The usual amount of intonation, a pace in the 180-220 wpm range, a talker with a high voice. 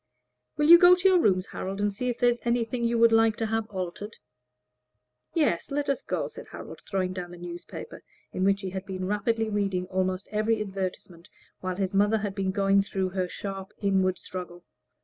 Yes: average, 3.3 semitones; average, 200 wpm; high, 200 Hz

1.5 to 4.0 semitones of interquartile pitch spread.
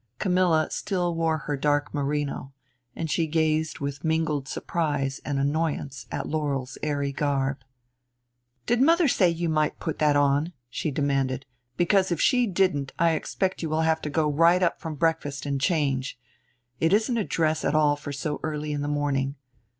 Yes: average, 2.7 semitones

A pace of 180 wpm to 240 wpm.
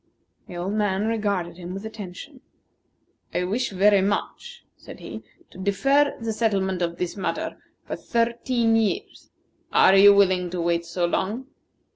No: average, 150 wpm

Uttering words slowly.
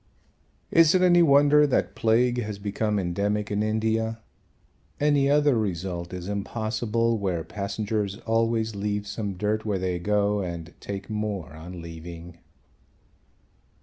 Yes: slow, 130 wpm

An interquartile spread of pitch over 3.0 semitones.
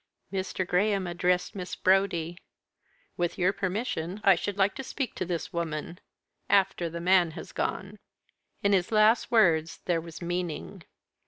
No: narrow, 2.5 semitones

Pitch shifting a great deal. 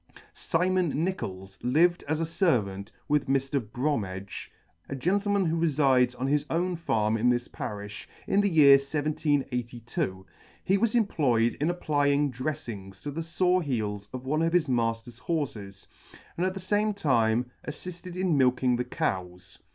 Yes: wide, 6.1 semitones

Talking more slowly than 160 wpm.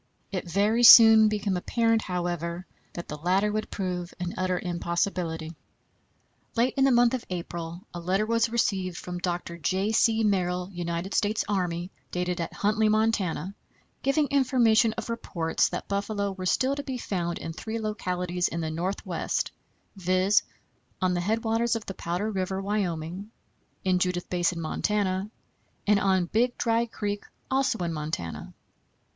Yes: average, 150 wpm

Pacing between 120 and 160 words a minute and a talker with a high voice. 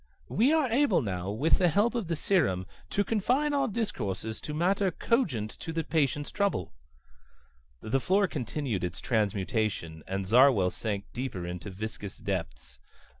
No: average, 150 wpm; low, 130 Hz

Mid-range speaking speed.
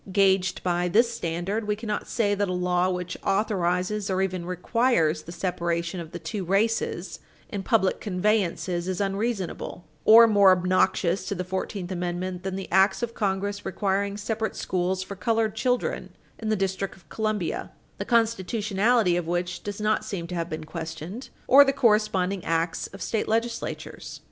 Yes: average, 165 wpm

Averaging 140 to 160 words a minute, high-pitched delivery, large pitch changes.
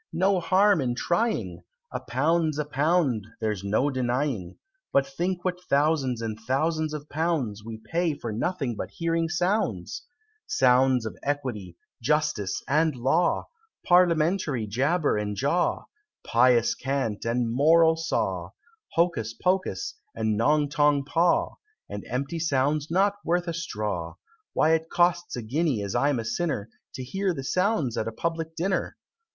No: average, 145 wpm; medium, 145 Hz; wide, 5.8 semitones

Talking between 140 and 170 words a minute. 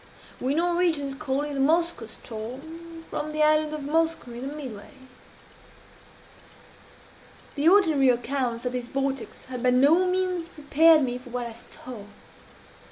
Yes: average, 145 wpm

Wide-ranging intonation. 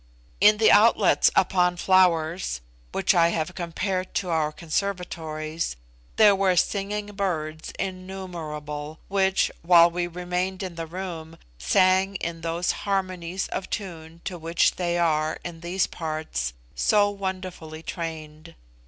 No: average, 2.8 semitones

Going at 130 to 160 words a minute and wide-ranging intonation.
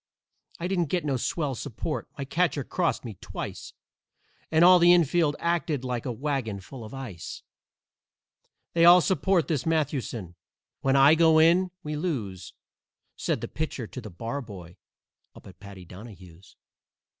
Yes: average, 150 wpm; wide, 7.1 semitones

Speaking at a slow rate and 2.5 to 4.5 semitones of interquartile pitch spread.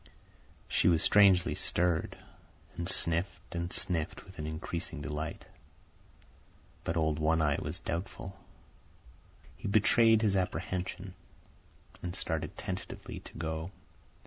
Yes: slow, 115 wpm; average, 2.8 semitones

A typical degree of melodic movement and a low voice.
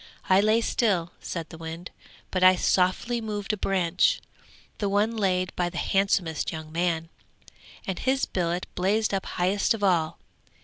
No: average, 3.0 semitones; medium, 185 Hz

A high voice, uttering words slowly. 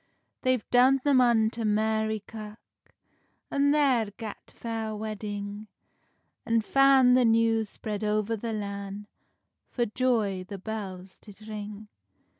Yes: high, 220 Hz; slow, 120 wpm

